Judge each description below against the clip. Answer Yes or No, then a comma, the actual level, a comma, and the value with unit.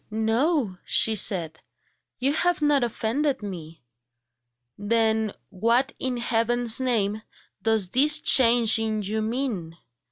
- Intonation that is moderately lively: Yes, average, 3.4 semitones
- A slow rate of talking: Yes, slow, 115 wpm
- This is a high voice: Yes, high, 225 Hz